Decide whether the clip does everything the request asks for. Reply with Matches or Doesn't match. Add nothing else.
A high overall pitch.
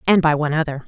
Doesn't match